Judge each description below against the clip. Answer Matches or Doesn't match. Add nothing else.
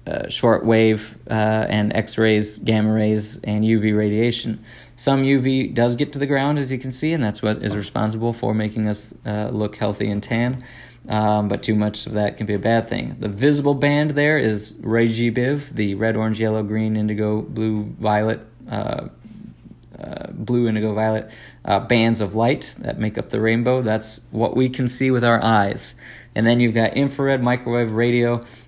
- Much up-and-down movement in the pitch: Doesn't match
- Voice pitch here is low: Matches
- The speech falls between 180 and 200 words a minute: Matches